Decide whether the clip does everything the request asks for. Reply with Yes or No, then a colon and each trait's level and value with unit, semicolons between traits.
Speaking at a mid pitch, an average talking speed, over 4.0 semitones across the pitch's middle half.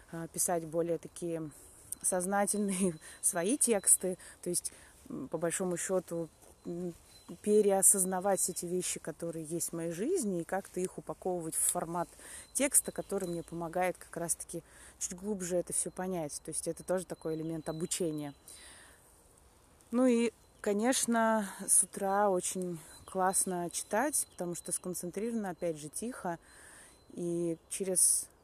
No: medium, 180 Hz; average, 125 wpm; narrow, 2.5 semitones